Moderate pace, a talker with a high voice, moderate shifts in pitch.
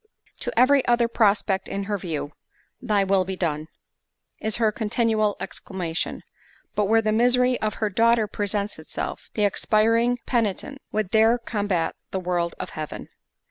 Yes: average, 150 wpm; high, 210 Hz; average, 3.3 semitones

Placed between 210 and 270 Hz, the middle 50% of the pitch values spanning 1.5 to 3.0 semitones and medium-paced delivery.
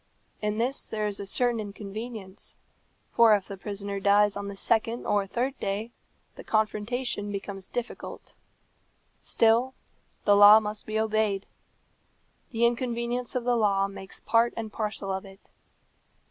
Yes: high, 215 Hz; narrow, 2.6 semitones; average, 145 wpm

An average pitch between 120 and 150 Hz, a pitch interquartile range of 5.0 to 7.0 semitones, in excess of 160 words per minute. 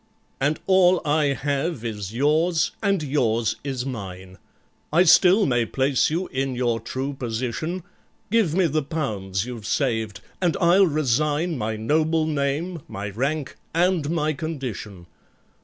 No: medium, 140 Hz; wide, 5.6 semitones; slow, 135 wpm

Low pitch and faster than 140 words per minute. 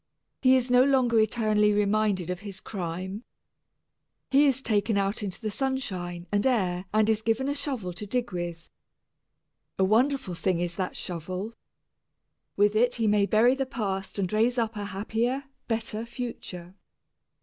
No: high, 215 Hz; average, 160 wpm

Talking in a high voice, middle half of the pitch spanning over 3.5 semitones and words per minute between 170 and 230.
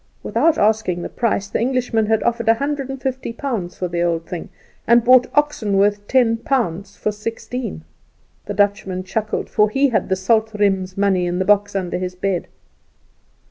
Yes: high, 210 Hz; average, 4.0 semitones; average, 180 wpm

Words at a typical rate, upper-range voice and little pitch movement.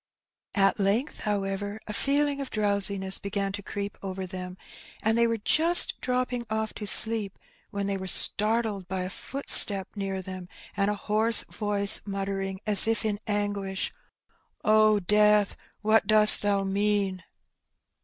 Yes: average, 145 wpm; high, 205 Hz; narrow, 1.9 semitones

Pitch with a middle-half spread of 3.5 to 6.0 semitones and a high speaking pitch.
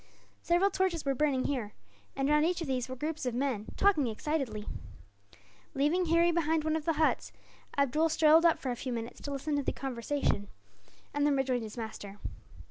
Yes: average, 4.1 semitones; very high, 285 Hz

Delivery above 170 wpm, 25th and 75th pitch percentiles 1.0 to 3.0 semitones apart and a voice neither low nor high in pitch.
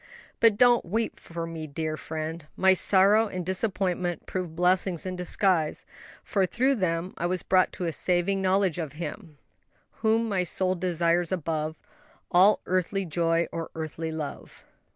No: average, 155 wpm; narrow, 2.5 semitones; medium, 180 Hz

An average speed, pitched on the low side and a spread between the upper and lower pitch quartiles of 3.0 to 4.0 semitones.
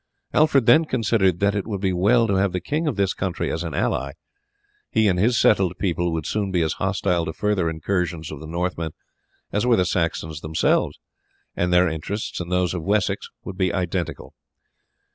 Yes: average, 195 wpm; very low, 90 Hz; average, 3.5 semitones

